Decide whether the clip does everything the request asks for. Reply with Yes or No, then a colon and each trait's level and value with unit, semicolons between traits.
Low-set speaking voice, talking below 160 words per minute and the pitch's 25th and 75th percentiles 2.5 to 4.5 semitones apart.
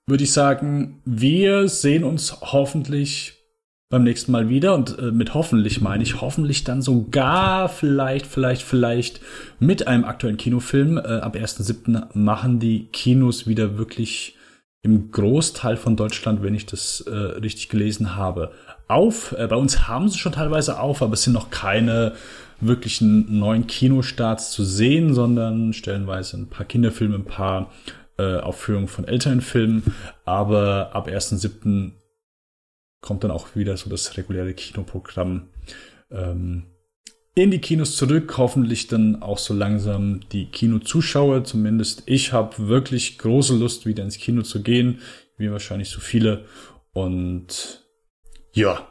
Yes: low, 115 Hz; average, 140 wpm; average, 4.1 semitones